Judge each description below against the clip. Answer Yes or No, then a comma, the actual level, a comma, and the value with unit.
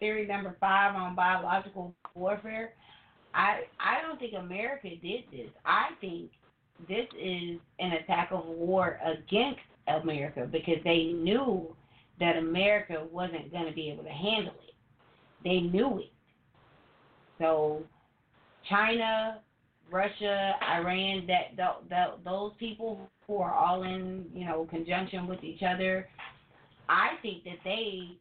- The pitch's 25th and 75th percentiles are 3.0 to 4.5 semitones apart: Yes, average, 3.5 semitones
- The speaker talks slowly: Yes, slow, 130 wpm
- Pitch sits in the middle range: Yes, medium, 180 Hz